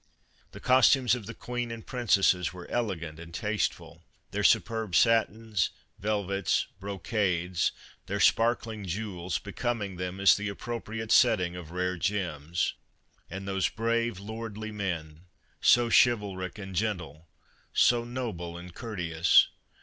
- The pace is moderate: No, slow, 125 wpm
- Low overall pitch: Yes, low, 100 Hz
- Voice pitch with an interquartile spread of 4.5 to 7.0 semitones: No, average, 4.1 semitones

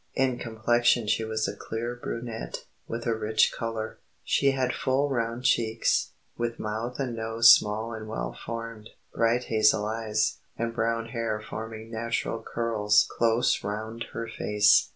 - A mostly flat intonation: Yes, narrow, 1.1 semitones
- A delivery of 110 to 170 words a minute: Yes, average, 150 wpm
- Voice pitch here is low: Yes, low, 115 Hz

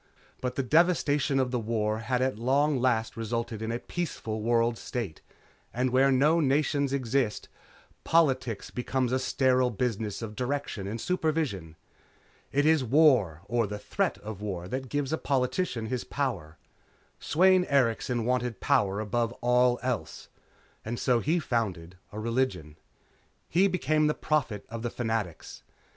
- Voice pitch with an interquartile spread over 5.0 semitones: No, average, 3.8 semitones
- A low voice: Yes, low, 125 Hz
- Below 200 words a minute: Yes, average, 150 wpm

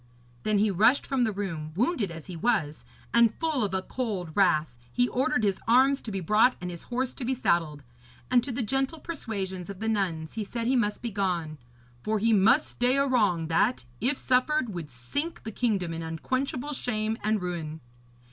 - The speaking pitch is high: Yes, high, 215 Hz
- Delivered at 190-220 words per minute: Yes, average, 200 wpm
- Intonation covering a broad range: Yes, wide, 5.8 semitones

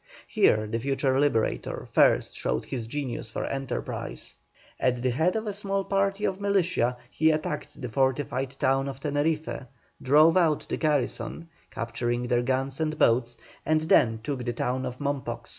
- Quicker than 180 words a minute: No, average, 160 wpm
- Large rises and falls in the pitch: No, average, 4.4 semitones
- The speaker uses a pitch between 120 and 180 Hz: Yes, low, 135 Hz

